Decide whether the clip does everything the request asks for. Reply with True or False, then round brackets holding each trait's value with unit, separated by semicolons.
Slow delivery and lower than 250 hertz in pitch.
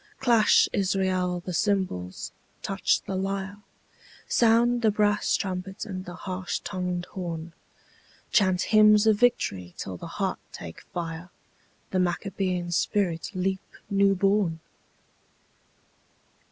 True (115 wpm; 190 Hz)